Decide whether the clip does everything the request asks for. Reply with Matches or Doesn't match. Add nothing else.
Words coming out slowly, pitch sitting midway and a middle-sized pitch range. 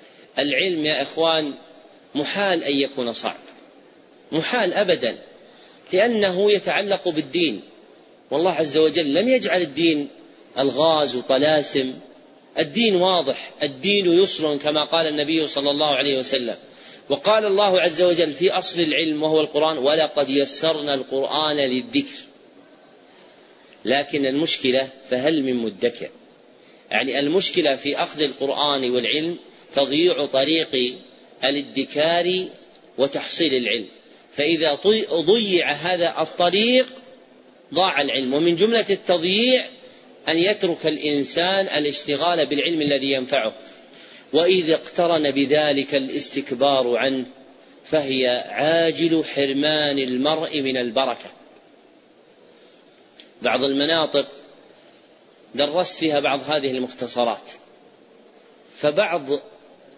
Doesn't match